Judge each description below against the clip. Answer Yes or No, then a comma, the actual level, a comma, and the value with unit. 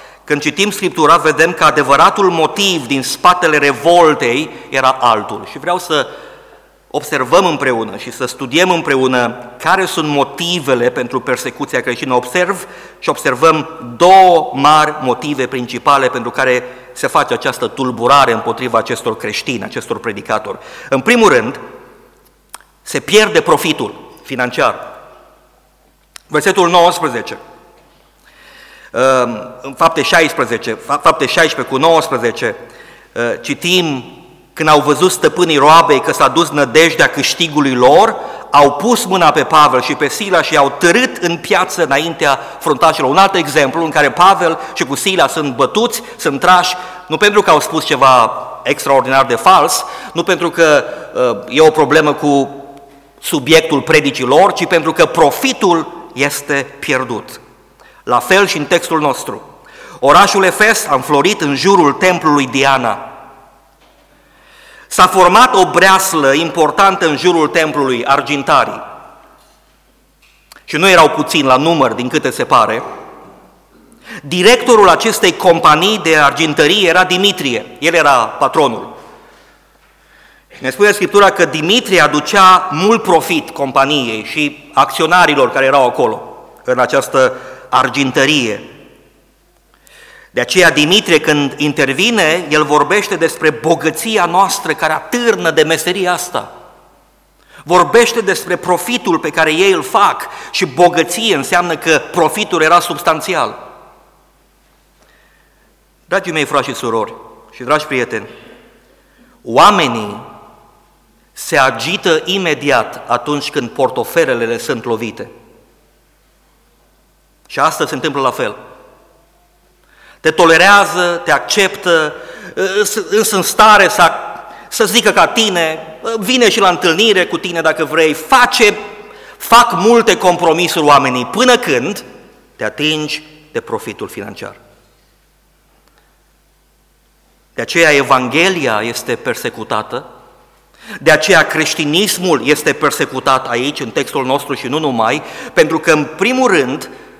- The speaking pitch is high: No, medium, 165 Hz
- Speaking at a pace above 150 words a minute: No, average, 120 wpm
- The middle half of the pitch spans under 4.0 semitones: No, average, 4.9 semitones